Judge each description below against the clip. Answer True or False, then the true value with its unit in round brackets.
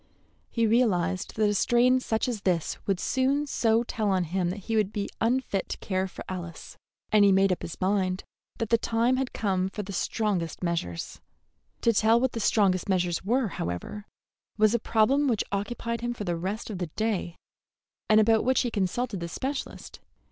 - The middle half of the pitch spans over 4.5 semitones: False (3.8 semitones)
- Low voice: False (210 Hz)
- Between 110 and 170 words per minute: False (190 wpm)